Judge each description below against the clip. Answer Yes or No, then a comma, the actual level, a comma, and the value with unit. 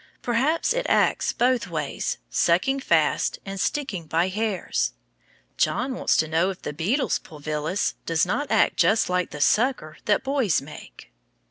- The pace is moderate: Yes, average, 150 wpm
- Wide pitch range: Yes, wide, 7.8 semitones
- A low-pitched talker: No, high, 190 Hz